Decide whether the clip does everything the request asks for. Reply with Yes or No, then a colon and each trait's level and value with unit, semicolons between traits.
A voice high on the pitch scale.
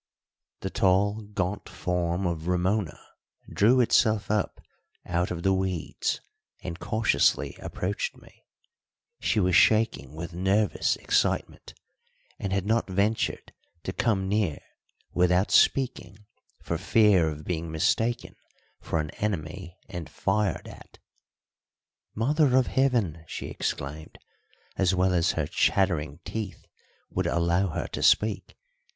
No: very low, 95 Hz